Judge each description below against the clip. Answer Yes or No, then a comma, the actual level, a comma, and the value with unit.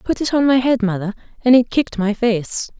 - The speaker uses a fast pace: Yes, fast, 235 wpm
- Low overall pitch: No, high, 230 Hz